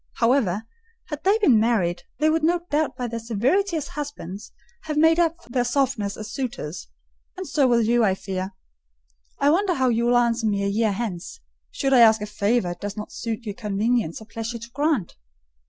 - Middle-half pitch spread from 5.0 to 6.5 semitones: Yes, wide, 5.6 semitones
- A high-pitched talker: Yes, high, 235 Hz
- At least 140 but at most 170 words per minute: No, fast, 205 wpm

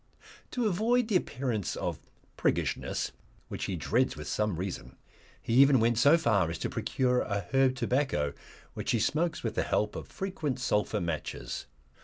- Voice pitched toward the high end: No, low, 120 Hz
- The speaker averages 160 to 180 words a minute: Yes, average, 165 wpm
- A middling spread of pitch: No, wide, 6.1 semitones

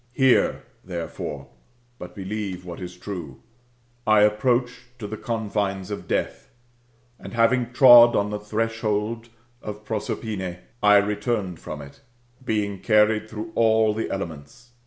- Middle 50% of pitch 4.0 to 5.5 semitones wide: No, average, 2.8 semitones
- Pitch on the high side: No, low, 105 Hz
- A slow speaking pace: Yes, slow, 130 wpm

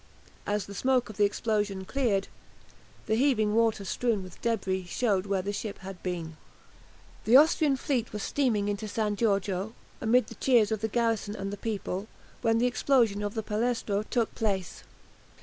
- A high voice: Yes, high, 215 Hz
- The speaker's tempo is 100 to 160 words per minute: No, average, 170 wpm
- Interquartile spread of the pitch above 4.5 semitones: No, average, 2.8 semitones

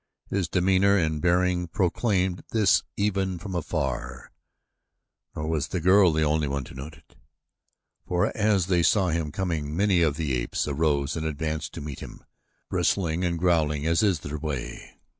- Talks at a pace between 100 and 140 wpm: No, average, 165 wpm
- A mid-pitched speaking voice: No, very low, 85 Hz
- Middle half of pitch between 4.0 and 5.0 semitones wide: No, average, 3.6 semitones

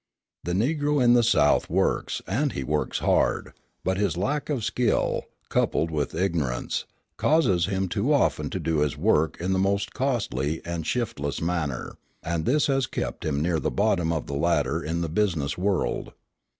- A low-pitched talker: Yes, very low, 90 Hz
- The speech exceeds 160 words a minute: Yes, average, 175 wpm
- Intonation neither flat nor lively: No, wide, 6.1 semitones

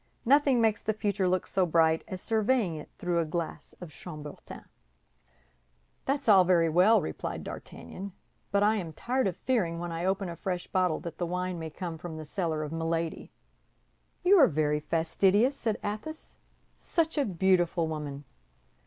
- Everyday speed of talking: Yes, average, 170 wpm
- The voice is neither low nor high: Yes, medium, 180 Hz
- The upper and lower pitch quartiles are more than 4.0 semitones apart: Yes, average, 4.4 semitones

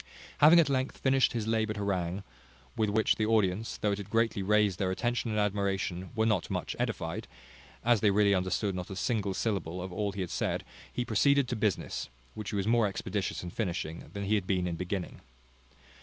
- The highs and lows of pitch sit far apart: No, average, 3.1 semitones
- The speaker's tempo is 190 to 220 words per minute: Yes, average, 200 wpm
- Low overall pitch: Yes, low, 105 Hz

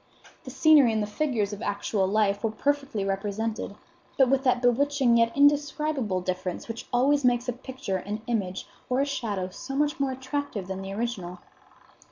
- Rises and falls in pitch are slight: No, average, 5.3 semitones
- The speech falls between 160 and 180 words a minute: Yes, average, 175 wpm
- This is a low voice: No, high, 235 Hz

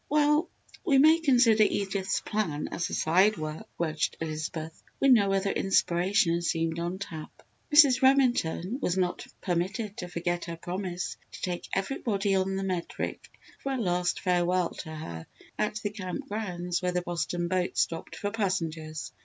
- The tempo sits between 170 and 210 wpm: No, average, 160 wpm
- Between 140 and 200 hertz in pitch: Yes, medium, 185 Hz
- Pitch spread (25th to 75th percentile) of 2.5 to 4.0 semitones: Yes, average, 3.6 semitones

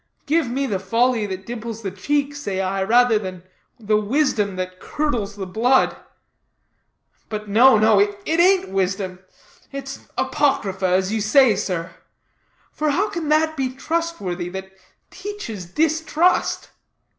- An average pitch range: No, wide, 7.0 semitones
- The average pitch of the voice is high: Yes, high, 220 Hz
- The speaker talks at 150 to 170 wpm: No, slow, 135 wpm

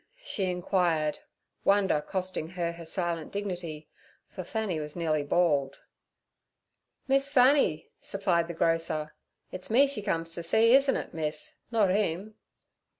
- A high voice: No, medium, 175 Hz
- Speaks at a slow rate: Yes, slow, 130 wpm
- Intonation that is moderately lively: Yes, average, 4.0 semitones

